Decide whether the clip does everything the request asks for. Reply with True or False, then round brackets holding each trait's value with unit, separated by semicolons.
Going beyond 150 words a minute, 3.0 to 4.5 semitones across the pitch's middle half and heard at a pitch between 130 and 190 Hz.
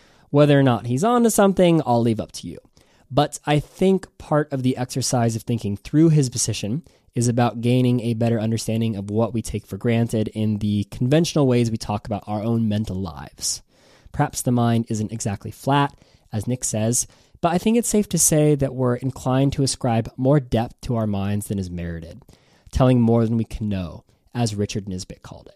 False (200 wpm; 4.1 semitones; 120 Hz)